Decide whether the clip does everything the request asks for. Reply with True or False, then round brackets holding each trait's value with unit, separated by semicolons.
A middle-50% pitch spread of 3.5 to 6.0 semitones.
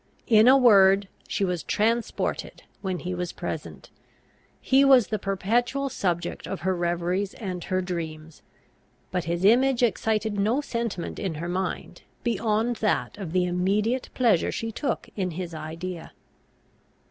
True (4.3 semitones)